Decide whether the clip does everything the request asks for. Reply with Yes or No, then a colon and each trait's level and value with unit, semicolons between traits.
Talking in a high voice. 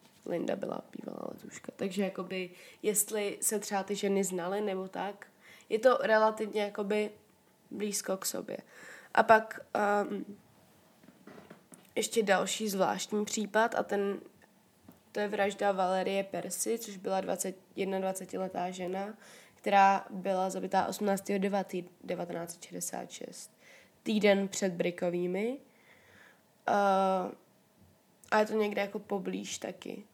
Yes: high, 200 Hz